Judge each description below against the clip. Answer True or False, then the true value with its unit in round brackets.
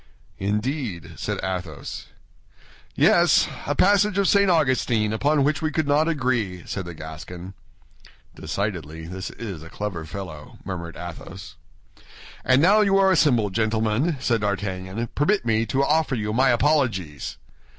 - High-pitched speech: False (110 Hz)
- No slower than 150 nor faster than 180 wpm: False (140 wpm)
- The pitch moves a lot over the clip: True (7.9 semitones)